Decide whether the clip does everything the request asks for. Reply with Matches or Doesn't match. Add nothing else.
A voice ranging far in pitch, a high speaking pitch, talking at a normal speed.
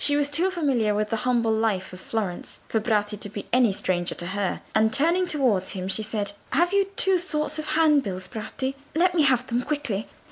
Doesn't match